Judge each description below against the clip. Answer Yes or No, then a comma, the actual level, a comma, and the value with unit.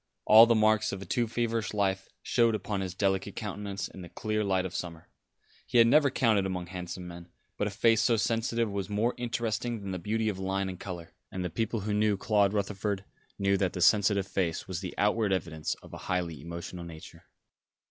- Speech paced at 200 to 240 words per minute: Yes, fast, 205 wpm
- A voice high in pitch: No, low, 100 Hz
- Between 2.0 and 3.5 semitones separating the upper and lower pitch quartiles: Yes, average, 2.8 semitones